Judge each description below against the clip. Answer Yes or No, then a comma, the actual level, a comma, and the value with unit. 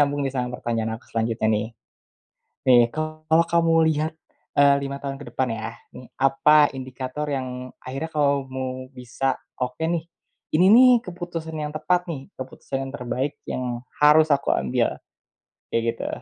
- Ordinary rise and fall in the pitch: Yes, average, 3.6 semitones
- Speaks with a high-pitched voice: No, low, 135 Hz